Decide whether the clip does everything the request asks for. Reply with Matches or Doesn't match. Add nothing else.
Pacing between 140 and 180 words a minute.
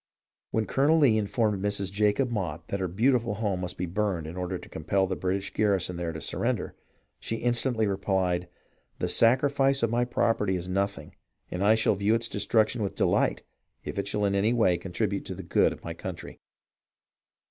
Doesn't match